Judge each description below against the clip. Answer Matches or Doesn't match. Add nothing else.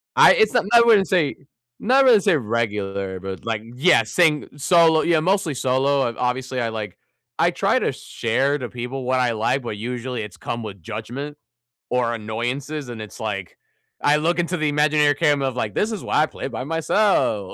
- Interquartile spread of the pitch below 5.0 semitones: Doesn't match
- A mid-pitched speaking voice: Doesn't match